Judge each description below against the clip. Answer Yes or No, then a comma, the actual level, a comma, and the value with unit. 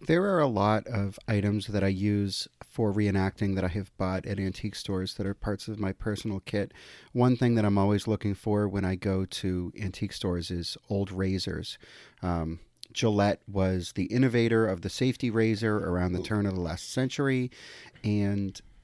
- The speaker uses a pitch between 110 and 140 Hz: No, low, 100 Hz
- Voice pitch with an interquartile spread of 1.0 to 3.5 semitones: Yes, average, 2.7 semitones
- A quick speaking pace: No, average, 185 wpm